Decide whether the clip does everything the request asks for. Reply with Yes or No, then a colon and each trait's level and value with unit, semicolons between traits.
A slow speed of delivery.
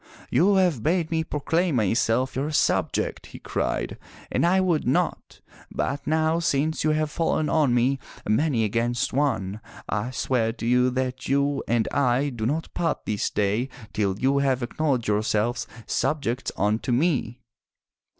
No: average, 150 wpm